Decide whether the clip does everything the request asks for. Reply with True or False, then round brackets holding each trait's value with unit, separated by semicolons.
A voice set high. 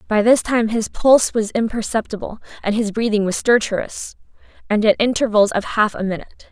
True (220 Hz)